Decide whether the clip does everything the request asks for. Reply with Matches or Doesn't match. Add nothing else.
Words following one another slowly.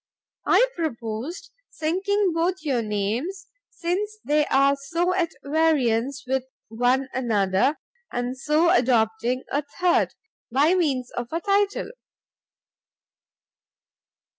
Matches